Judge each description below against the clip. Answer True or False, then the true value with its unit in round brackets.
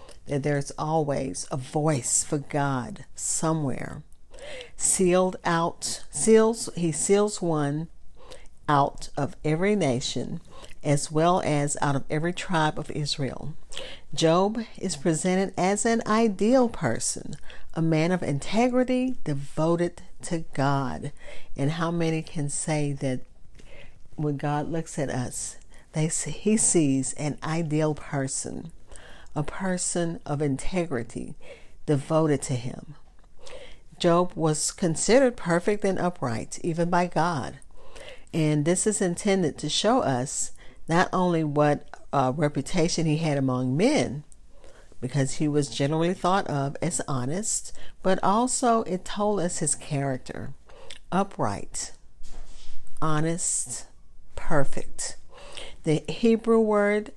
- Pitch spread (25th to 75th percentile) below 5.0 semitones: True (4.5 semitones)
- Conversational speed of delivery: False (120 wpm)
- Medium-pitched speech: True (160 Hz)